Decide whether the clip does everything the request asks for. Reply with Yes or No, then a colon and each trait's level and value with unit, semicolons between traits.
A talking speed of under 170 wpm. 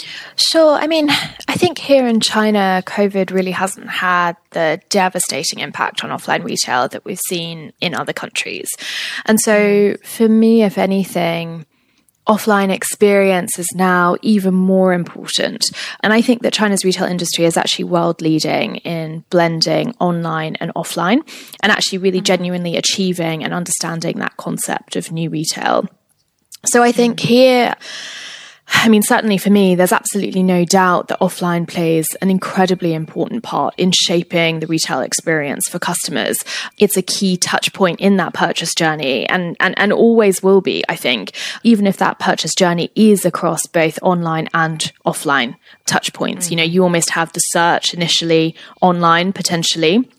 Yes: average, 160 wpm